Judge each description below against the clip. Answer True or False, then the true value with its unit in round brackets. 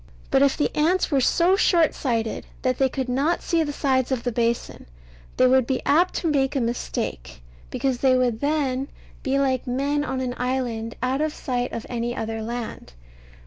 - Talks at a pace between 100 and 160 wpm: False (190 wpm)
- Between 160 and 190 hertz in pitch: False (260 Hz)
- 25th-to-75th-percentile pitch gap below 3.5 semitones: True (2.8 semitones)